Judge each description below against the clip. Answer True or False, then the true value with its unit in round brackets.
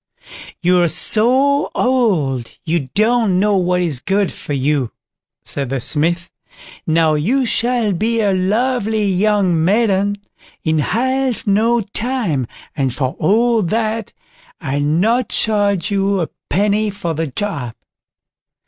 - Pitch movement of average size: False (5.7 semitones)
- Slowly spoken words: True (125 wpm)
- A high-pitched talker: True (200 Hz)